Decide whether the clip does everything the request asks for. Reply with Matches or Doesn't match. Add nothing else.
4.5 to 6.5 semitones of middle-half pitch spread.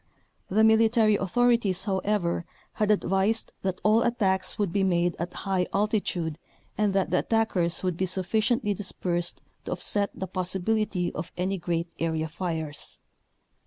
Doesn't match